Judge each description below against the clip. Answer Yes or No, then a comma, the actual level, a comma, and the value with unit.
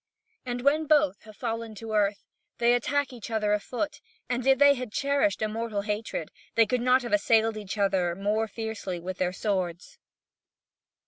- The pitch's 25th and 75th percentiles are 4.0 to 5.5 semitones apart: No, average, 3.5 semitones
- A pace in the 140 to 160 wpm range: No, average, 175 wpm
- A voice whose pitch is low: No, high, 220 Hz